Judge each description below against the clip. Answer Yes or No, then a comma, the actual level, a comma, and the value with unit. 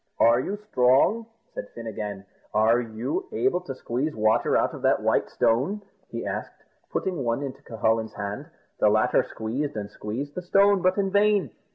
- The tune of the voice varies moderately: No, wide, 8.9 semitones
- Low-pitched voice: Yes, low, 130 Hz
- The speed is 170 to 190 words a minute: Yes, average, 175 wpm